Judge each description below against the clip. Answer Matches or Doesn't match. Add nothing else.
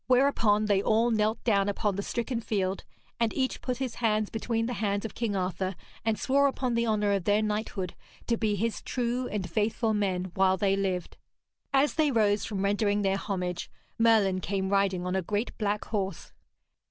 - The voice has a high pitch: Matches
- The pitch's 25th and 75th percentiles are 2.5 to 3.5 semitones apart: Matches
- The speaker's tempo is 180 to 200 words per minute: Matches